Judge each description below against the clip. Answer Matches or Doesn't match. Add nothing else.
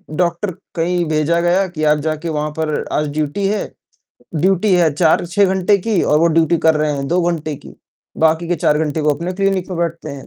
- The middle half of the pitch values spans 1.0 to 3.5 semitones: Matches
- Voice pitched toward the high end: Doesn't match